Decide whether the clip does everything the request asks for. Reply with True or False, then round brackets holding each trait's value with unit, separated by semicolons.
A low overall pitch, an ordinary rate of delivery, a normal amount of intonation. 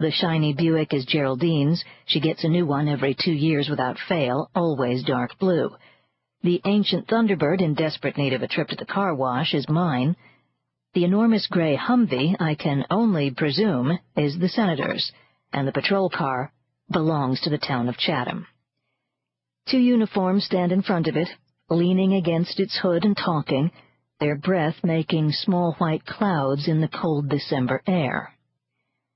False (160 Hz; 160 wpm; 4.3 semitones)